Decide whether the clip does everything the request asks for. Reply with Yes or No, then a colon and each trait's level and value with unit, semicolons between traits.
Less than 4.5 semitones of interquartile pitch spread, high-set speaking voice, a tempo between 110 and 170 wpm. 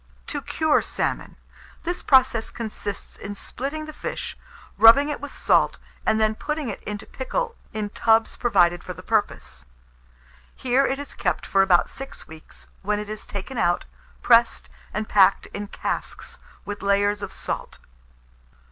No: average, 4.9 semitones; high, 220 Hz; average, 155 wpm